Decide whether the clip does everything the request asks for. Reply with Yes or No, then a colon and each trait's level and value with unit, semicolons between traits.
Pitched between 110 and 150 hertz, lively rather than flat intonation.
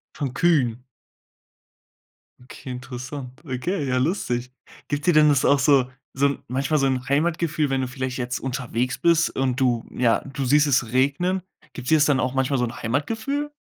No: low, 135 Hz; average, 2.9 semitones